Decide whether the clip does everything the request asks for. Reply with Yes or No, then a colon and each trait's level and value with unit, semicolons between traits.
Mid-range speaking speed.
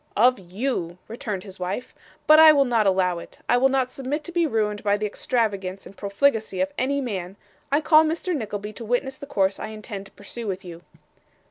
No: fast, 210 wpm